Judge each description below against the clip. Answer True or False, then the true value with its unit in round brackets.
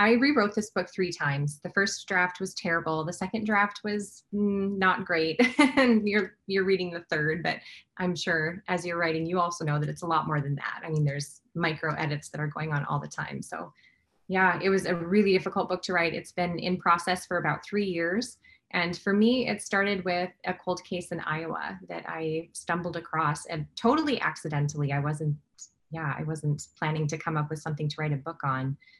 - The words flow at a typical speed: False (215 wpm)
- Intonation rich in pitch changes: False (3.8 semitones)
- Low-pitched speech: False (175 Hz)